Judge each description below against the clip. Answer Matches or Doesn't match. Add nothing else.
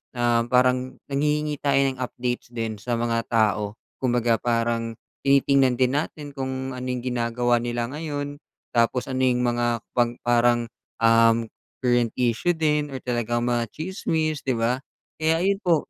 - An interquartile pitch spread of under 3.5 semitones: Matches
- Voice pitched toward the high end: Doesn't match